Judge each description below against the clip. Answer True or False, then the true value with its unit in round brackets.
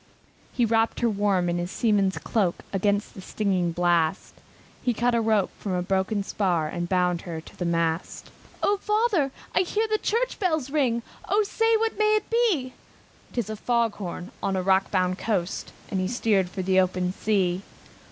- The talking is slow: False (185 wpm)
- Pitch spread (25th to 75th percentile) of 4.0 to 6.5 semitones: True (5.6 semitones)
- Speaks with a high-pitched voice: True (200 Hz)